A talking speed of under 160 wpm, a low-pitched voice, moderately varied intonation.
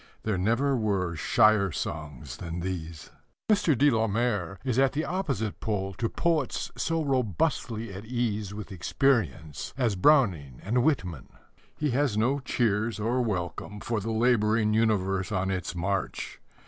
Yes: average, 150 wpm; low, 110 Hz; average, 4.7 semitones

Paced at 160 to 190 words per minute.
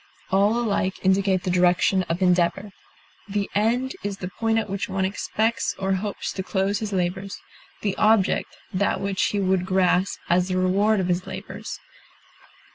Yes: average, 165 wpm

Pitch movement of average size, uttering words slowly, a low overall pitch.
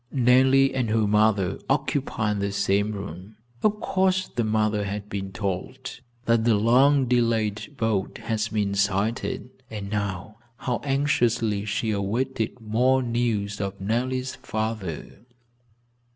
Yes: average, 3.6 semitones; slow, 125 wpm; low, 110 Hz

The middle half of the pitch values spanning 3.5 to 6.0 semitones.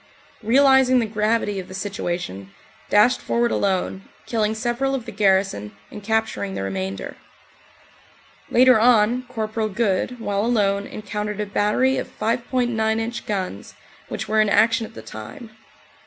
No: average, 3.0 semitones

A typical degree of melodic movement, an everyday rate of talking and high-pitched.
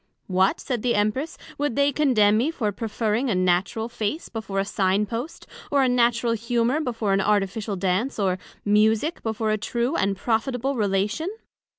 Yes: average, 3.4 semitones; average, 170 wpm; high, 220 Hz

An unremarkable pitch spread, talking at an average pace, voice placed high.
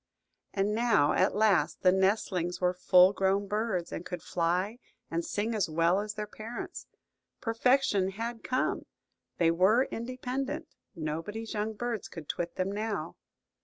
Yes: average, 3.8 semitones; average, 145 wpm; high, 205 Hz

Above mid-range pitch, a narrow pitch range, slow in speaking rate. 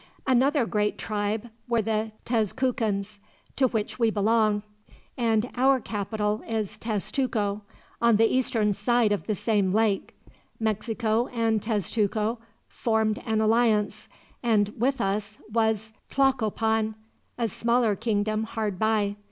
Yes: high, 220 Hz; narrow, 1.8 semitones; slow, 120 wpm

